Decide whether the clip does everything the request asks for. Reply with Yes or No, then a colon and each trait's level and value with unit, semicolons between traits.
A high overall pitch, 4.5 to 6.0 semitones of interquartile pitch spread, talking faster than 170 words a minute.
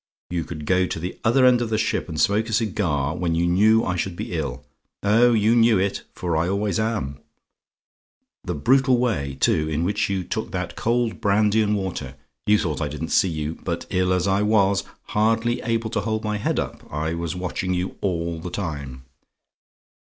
No: very low, 95 Hz; average, 4.8 semitones; average, 200 wpm